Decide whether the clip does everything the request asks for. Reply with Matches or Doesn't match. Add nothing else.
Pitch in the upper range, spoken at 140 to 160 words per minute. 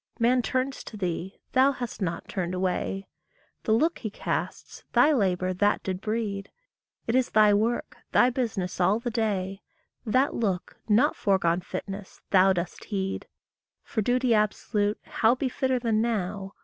Matches